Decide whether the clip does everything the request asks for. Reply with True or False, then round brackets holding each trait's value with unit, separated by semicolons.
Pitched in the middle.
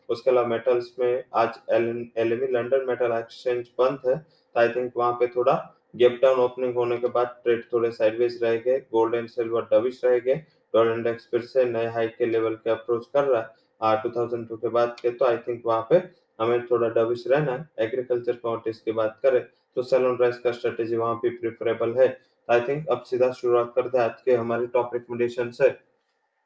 False (120 Hz)